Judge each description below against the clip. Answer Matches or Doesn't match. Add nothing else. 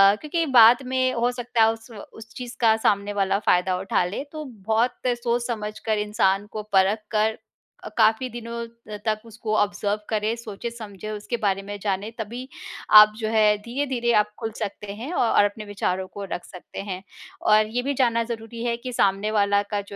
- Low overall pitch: Doesn't match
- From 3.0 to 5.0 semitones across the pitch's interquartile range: Doesn't match